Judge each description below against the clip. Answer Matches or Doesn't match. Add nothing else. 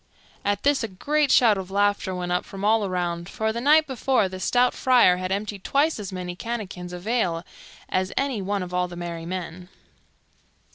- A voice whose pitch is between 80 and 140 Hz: Doesn't match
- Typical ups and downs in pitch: Matches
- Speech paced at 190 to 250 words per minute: Matches